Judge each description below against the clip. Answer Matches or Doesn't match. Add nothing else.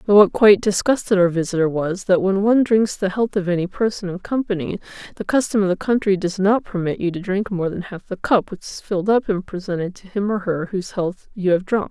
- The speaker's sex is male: Doesn't match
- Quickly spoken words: Matches